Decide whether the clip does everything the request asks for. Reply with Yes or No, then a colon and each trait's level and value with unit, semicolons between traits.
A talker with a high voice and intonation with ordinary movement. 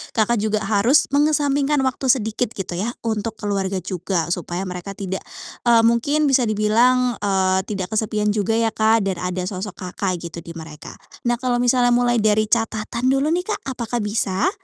Yes: high, 220 Hz; average, 4.0 semitones